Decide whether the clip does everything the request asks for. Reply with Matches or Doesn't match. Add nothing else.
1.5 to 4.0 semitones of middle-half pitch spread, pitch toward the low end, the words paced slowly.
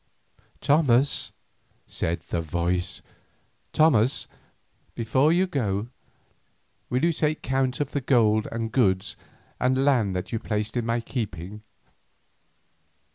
Doesn't match